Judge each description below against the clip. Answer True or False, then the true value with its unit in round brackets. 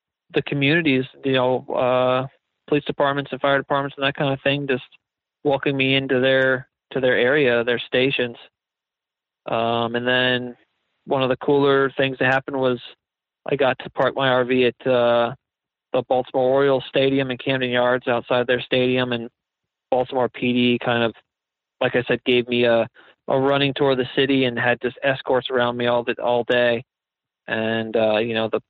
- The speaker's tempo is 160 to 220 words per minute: True (185 wpm)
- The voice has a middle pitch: False (130 Hz)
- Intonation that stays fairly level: True (2.0 semitones)